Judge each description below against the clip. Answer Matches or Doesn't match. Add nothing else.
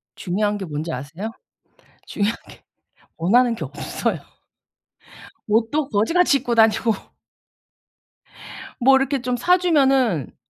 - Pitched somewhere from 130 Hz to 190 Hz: Doesn't match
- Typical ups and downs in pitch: Matches